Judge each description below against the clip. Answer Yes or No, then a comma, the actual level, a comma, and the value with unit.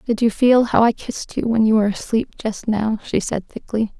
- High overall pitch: Yes, high, 220 Hz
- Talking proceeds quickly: Yes, fast, 240 wpm